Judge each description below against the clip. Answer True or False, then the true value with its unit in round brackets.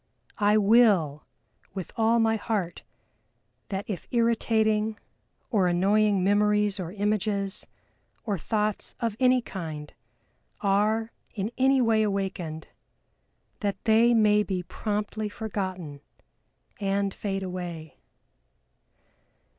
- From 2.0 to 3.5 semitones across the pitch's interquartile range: True (2.4 semitones)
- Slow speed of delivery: True (100 wpm)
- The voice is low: False (205 Hz)